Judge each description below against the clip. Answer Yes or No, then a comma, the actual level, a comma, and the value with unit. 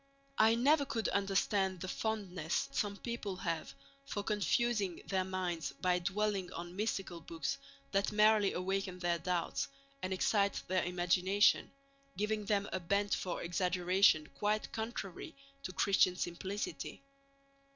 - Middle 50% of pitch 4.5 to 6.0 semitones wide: No, narrow, 2.6 semitones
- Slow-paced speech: Yes, slow, 130 wpm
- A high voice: Yes, high, 195 Hz